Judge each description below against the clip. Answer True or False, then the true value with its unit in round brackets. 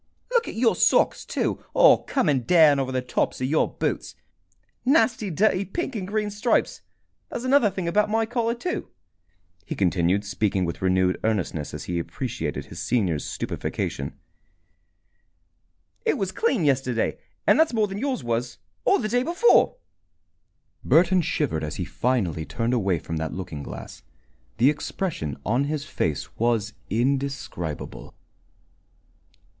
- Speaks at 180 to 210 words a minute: False (145 wpm)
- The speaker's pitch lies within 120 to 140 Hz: True (135 Hz)